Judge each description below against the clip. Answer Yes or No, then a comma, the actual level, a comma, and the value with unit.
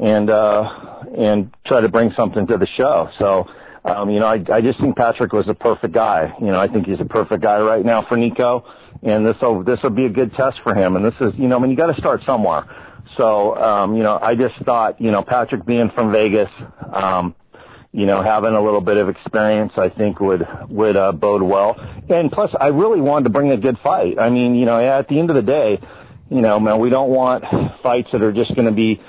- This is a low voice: Yes, low, 110 Hz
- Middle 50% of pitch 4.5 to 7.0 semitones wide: No, average, 2.8 semitones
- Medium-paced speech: No, fast, 250 wpm